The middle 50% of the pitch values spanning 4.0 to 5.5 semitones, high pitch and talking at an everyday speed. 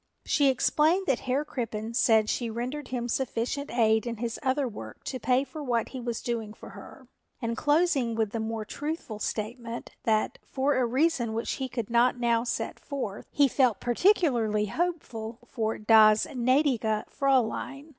No: average, 3.5 semitones; high, 240 Hz; average, 165 wpm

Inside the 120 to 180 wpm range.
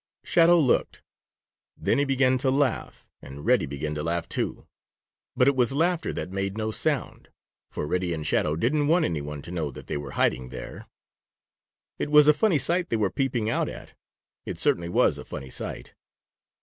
No: average, 190 wpm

